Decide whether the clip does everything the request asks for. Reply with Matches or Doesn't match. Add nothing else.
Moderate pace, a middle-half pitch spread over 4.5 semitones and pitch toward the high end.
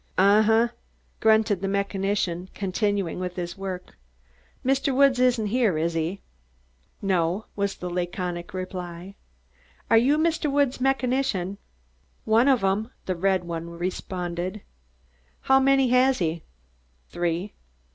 Doesn't match